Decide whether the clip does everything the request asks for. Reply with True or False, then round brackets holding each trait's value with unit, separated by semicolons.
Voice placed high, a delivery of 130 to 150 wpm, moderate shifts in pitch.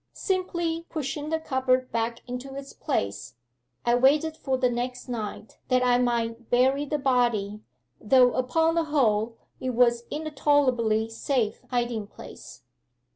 True (250 Hz; 145 wpm; 3.4 semitones)